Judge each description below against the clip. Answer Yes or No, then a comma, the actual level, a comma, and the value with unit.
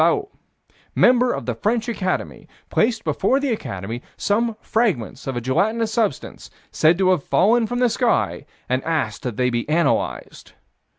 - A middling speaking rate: Yes, average, 160 wpm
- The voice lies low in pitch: No, high, 205 Hz